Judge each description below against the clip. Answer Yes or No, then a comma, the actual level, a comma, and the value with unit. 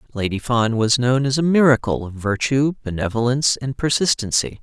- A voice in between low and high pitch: No, low, 125 Hz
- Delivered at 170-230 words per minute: No, average, 155 wpm